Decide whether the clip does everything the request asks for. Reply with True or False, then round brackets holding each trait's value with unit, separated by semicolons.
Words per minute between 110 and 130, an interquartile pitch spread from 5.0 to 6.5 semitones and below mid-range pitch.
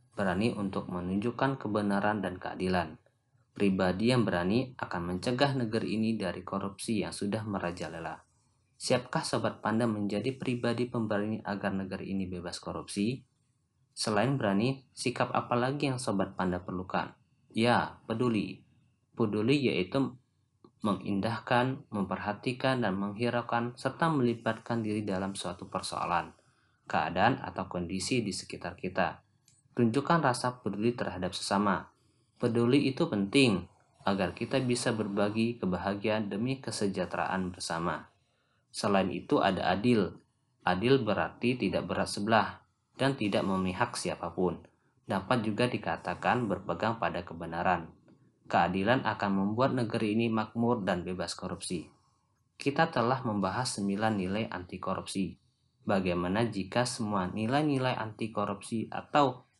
False (115 wpm; 4.2 semitones; 110 Hz)